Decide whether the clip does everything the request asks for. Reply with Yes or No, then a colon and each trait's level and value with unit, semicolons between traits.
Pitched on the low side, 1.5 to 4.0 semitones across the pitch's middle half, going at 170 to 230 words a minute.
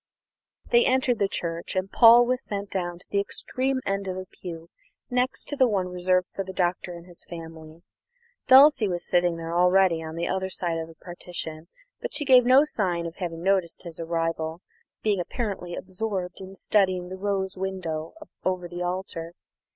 No: medium, 185 Hz; average, 2.8 semitones; average, 180 wpm